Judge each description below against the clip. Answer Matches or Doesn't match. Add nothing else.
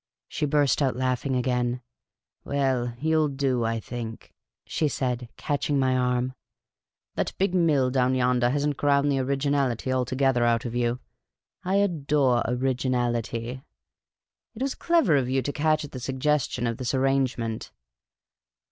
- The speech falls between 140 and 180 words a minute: Matches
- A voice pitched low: Matches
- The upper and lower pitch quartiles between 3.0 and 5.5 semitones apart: Doesn't match